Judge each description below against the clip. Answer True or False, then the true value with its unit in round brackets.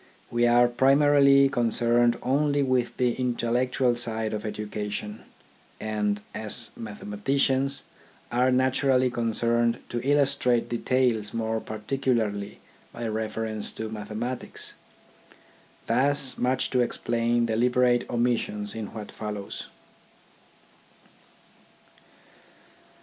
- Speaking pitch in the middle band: False (120 Hz)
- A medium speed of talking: False (90 wpm)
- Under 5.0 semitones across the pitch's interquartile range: True (2.7 semitones)